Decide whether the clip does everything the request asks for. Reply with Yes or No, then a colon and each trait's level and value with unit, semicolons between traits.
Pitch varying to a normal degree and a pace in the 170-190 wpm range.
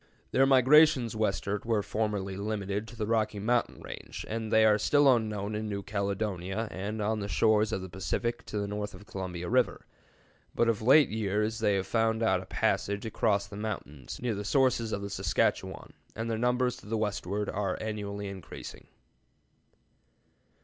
No: narrow, 2.1 semitones; average, 175 wpm